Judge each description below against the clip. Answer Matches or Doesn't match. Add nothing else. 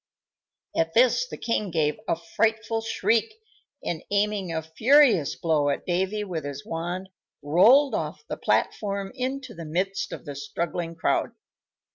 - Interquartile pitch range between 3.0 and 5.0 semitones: Doesn't match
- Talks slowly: Doesn't match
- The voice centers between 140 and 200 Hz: Matches